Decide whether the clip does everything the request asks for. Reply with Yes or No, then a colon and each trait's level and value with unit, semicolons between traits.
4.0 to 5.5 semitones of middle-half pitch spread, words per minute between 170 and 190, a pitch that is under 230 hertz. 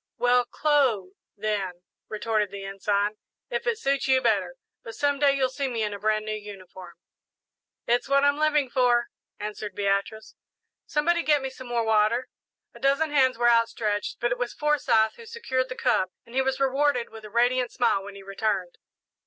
No: average, 4.3 semitones; average, 185 wpm; high, 240 Hz